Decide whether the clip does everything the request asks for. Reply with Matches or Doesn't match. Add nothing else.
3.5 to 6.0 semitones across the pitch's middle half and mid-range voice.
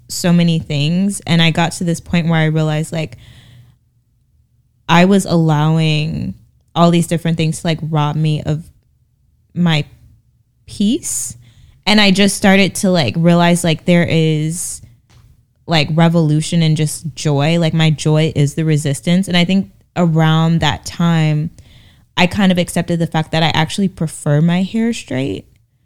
Matches